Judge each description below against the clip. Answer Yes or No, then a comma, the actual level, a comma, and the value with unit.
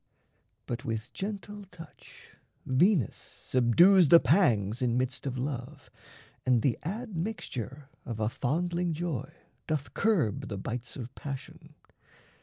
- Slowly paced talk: Yes, slow, 120 wpm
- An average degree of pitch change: No, wide, 6.3 semitones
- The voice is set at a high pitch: No, medium, 140 Hz